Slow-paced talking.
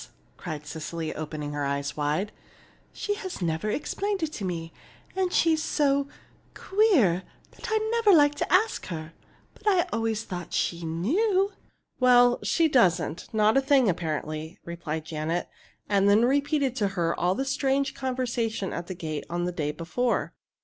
No: average, 160 wpm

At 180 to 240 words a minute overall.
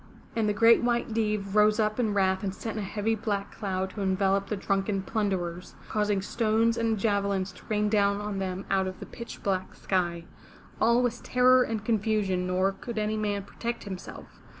Yes: average, 190 wpm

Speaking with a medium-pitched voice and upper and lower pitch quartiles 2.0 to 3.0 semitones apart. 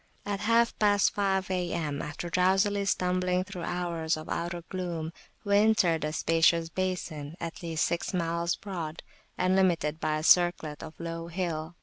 Yes: medium, 175 Hz; narrow, 2.4 semitones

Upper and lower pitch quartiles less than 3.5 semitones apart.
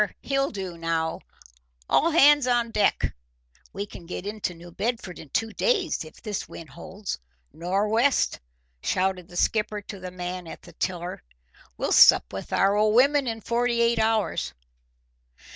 No: average, 4.6 semitones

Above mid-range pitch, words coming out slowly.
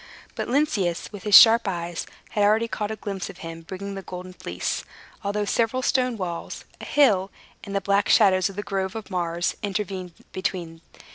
No: high, 195 Hz; average, 185 wpm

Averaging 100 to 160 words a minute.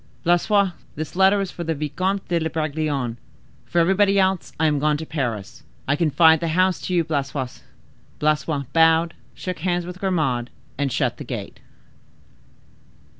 Yes: average, 150 wpm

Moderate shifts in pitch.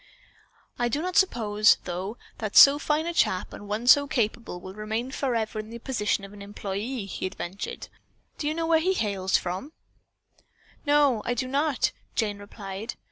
No: wide, 5.7 semitones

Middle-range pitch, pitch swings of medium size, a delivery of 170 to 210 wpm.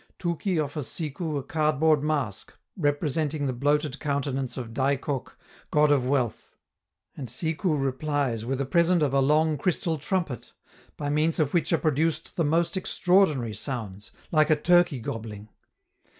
No: medium, 145 Hz; average, 3.2 semitones; average, 150 wpm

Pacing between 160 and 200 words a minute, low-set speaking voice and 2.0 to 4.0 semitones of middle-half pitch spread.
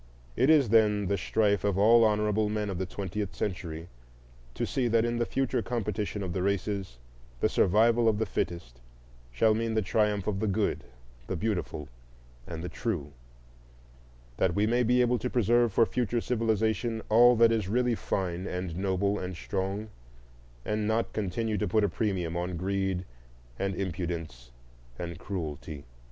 Yes: average, 165 wpm; low, 105 Hz; average, 3.7 semitones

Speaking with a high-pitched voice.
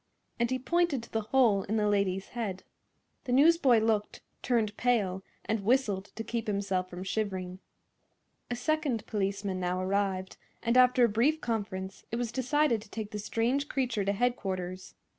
Yes: high, 220 Hz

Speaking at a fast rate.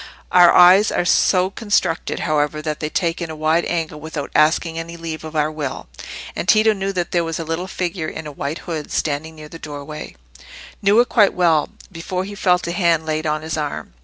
Yes: fast, 210 wpm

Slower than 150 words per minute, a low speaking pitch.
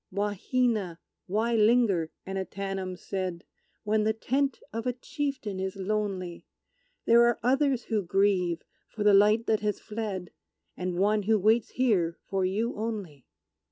No: average, 140 wpm; high, 210 Hz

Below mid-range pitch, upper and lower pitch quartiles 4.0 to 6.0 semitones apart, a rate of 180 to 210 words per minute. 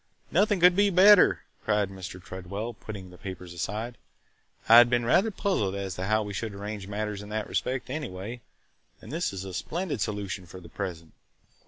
Yes: low, 105 Hz; average, 4.3 semitones; average, 185 wpm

